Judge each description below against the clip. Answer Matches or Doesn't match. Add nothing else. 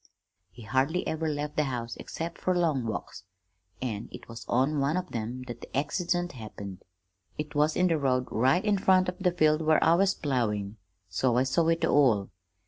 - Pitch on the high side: Doesn't match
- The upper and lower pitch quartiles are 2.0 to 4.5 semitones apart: Doesn't match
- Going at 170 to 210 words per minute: Matches